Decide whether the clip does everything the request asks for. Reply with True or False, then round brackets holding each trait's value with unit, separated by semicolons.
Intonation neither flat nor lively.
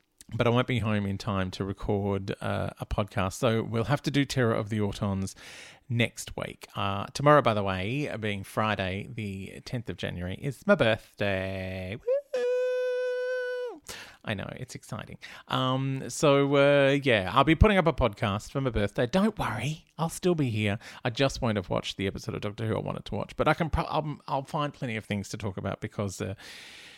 False (6.0 semitones)